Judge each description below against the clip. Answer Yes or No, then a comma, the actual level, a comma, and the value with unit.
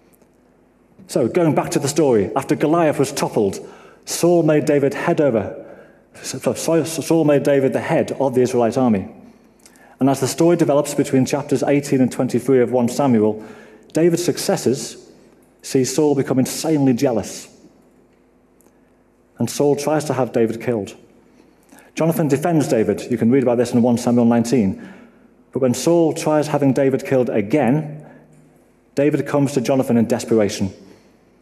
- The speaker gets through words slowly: No, average, 145 wpm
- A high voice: No, low, 135 Hz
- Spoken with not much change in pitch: No, average, 3.3 semitones